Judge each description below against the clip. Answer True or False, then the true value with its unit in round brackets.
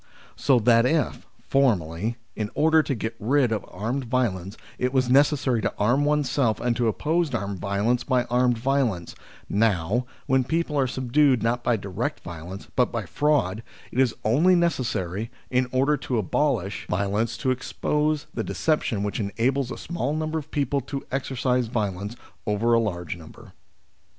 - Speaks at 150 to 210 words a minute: True (160 wpm)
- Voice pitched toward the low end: True (120 Hz)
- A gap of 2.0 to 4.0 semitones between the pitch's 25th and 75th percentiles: False (4.7 semitones)